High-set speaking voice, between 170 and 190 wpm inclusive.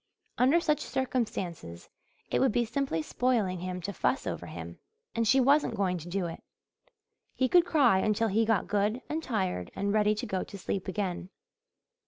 Yes: high, 210 Hz; average, 180 wpm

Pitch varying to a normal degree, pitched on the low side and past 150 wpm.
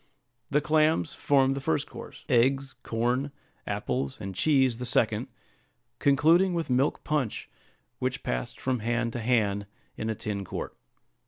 No: average, 4.3 semitones; low, 125 Hz; average, 145 wpm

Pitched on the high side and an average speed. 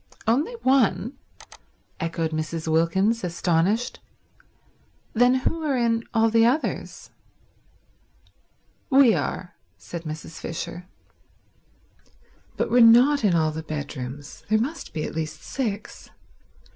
No: high, 200 Hz; slow, 110 wpm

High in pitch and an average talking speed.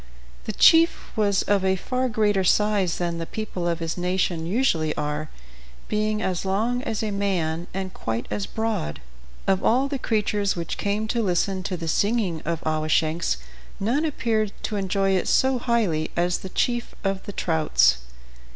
Yes: high, 195 Hz; average, 170 wpm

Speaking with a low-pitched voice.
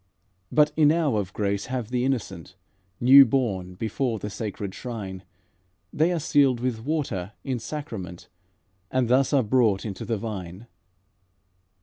Yes: low, 115 Hz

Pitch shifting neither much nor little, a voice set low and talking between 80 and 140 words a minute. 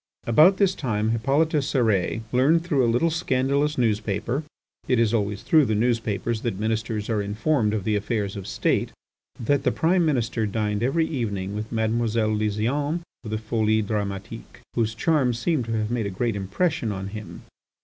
No: average, 4.3 semitones; low, 115 Hz; average, 170 wpm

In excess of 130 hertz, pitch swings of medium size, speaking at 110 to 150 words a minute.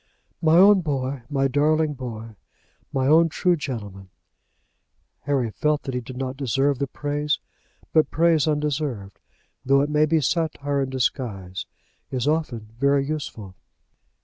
Yes: medium, 140 Hz; average, 3.1 semitones; average, 140 wpm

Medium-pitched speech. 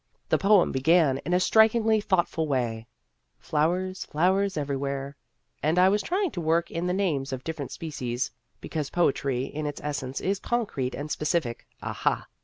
Yes: medium, 160 Hz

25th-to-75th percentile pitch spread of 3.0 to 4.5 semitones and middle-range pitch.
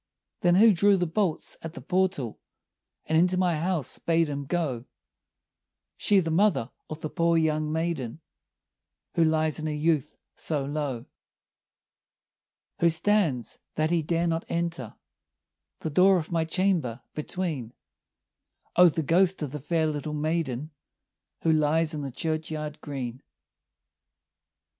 No: narrow, 2.5 semitones; medium, 160 Hz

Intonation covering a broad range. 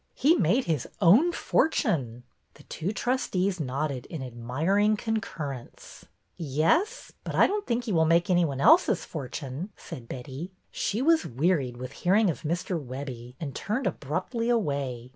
Yes: wide, 8.3 semitones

